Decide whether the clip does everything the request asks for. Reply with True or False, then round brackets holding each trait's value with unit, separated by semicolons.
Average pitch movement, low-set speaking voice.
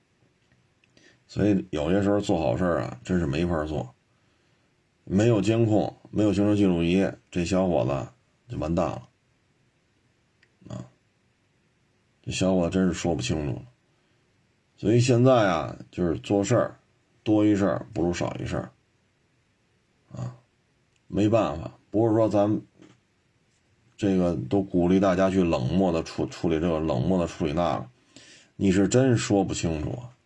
True (3.9 semitones; 95 Hz)